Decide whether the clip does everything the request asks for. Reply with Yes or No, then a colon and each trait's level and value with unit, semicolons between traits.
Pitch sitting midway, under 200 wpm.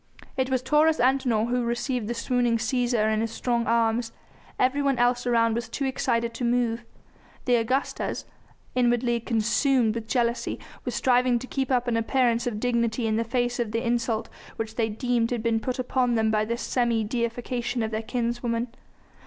No: high, 240 Hz; average, 180 wpm